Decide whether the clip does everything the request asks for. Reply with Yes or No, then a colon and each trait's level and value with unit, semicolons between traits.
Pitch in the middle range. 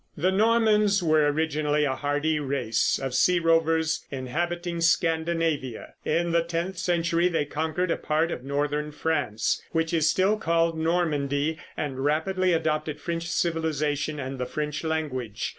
Yes: medium, 160 Hz